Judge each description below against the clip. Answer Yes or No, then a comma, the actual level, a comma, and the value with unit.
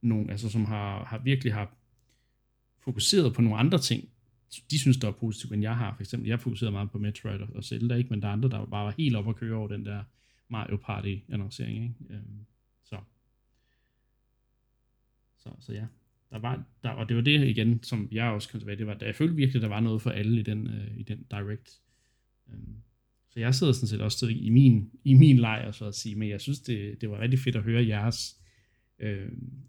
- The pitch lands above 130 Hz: No, low, 115 Hz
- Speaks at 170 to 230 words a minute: Yes, average, 220 wpm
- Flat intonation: Yes, narrow, 2.2 semitones